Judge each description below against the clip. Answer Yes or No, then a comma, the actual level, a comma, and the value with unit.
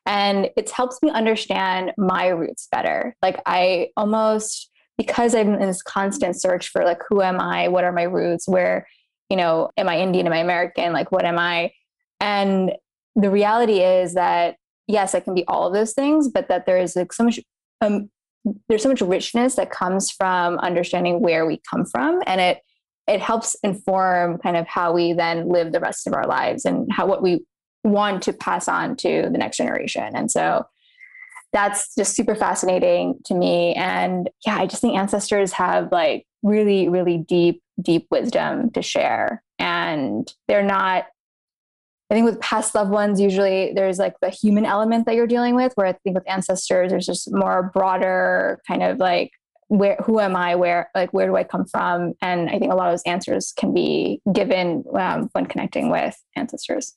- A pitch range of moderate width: Yes, average, 3.3 semitones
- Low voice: No, high, 195 Hz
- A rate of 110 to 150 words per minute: No, average, 190 wpm